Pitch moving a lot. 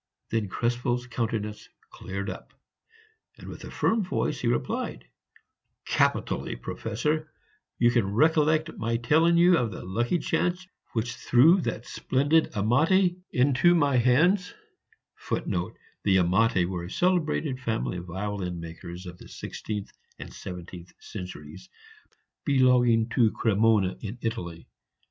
Yes: wide, 7.5 semitones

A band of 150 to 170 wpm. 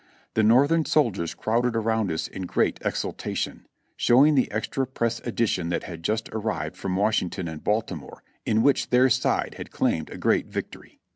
Yes: average, 165 wpm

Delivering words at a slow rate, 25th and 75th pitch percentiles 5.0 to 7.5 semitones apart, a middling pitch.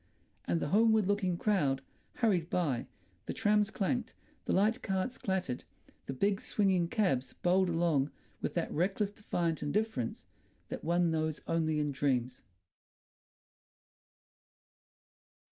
Yes: slow, 120 wpm; wide, 5.6 semitones; medium, 180 Hz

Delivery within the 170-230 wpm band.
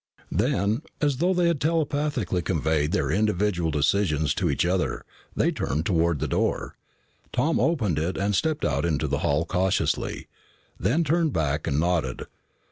No: average, 155 wpm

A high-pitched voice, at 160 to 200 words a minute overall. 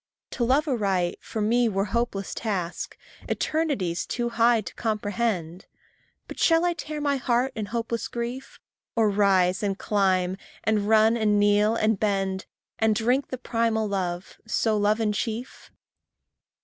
No: high, 220 Hz; average, 150 wpm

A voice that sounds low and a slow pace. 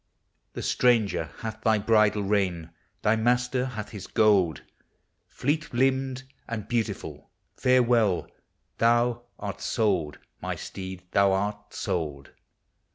Yes: low, 110 Hz; slow, 125 wpm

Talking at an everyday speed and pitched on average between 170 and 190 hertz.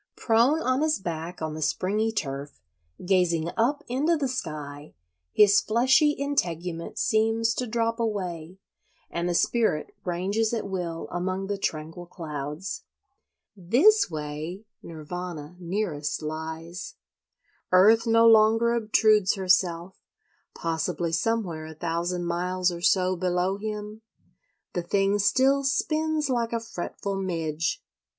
No: slow, 120 wpm; medium, 185 Hz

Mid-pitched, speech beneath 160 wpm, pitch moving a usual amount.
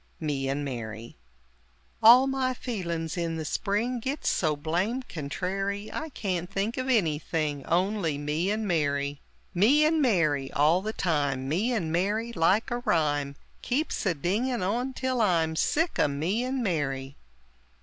No: medium, 180 Hz; average, 150 wpm; wide, 7.7 semitones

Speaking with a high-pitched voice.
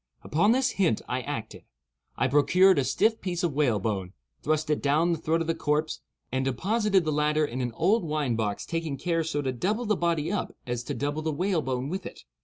No: medium, 155 Hz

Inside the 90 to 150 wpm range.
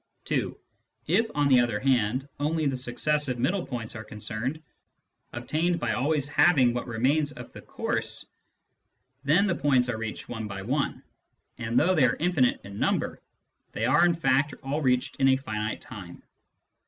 No: average, 165 wpm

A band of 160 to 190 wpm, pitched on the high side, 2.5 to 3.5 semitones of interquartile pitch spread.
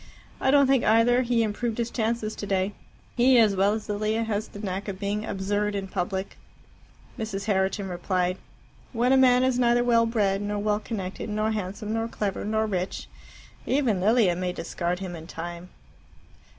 Yes: average, 175 wpm; high, 210 Hz; average, 3.1 semitones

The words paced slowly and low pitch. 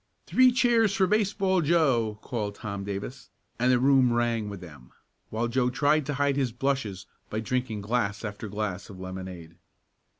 No: average, 165 wpm; low, 120 Hz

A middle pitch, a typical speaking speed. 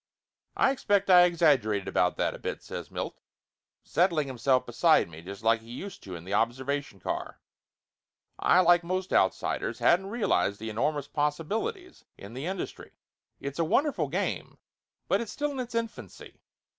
Yes: medium, 150 Hz; average, 170 wpm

